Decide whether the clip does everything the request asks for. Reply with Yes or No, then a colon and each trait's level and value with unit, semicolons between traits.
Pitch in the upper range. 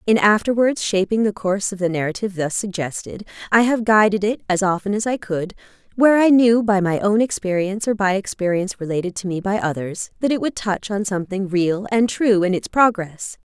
Yes: high, 200 Hz